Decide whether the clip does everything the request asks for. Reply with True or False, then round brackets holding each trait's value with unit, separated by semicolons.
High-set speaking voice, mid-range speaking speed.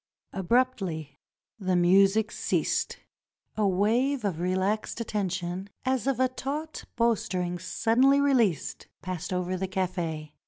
False (195 Hz; 125 wpm)